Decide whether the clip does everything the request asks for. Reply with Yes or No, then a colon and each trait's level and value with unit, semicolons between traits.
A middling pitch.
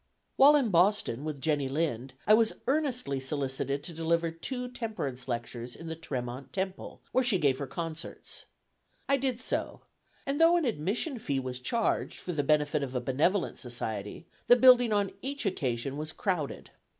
Yes: medium, 160 Hz